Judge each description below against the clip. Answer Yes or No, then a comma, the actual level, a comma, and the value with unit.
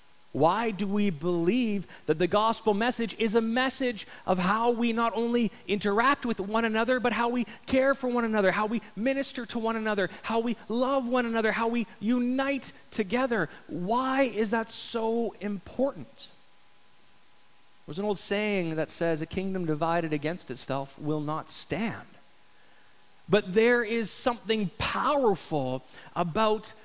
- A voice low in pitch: No, high, 220 Hz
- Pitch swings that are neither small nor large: Yes, average, 4.0 semitones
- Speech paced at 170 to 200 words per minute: No, average, 150 wpm